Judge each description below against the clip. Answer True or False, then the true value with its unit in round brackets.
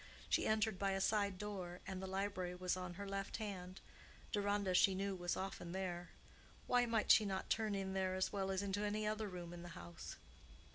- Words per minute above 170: True (205 wpm)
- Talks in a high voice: True (195 Hz)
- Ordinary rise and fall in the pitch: False (1.9 semitones)